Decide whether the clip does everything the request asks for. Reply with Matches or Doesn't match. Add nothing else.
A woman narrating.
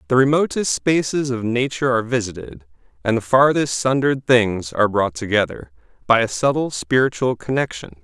Doesn't match